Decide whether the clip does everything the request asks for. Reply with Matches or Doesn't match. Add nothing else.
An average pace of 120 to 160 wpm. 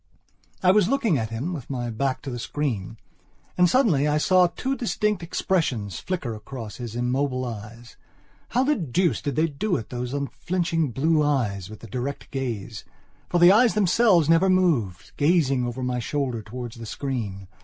Doesn't match